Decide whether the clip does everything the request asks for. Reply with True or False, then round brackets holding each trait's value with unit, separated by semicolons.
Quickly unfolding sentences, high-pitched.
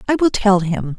True (245 wpm; 200 Hz)